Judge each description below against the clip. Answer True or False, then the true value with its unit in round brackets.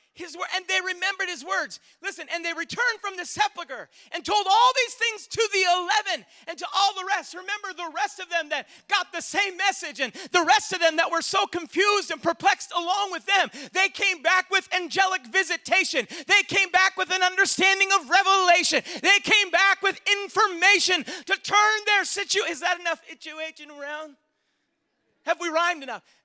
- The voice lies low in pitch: False (370 Hz)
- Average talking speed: True (190 wpm)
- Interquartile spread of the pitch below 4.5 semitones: True (2.8 semitones)